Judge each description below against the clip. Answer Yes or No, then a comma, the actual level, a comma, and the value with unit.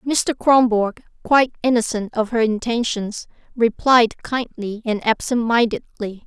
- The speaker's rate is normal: No, slow, 115 wpm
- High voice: Yes, high, 230 Hz